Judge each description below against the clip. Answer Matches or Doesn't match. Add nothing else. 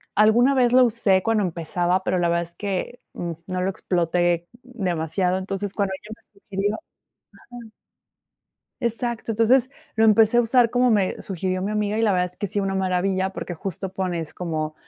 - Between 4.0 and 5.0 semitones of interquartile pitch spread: Doesn't match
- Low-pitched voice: Doesn't match